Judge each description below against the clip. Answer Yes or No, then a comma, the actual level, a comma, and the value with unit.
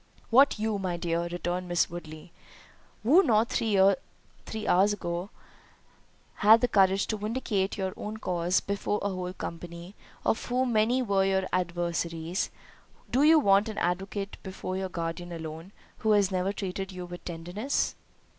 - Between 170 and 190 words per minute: No, average, 150 wpm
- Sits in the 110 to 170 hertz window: No, high, 190 Hz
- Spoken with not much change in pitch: No, average, 3.4 semitones